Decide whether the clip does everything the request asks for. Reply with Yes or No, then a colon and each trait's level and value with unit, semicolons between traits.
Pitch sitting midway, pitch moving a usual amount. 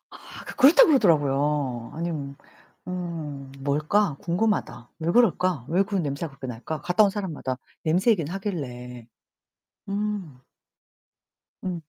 No: medium, 165 Hz; wide, 5.7 semitones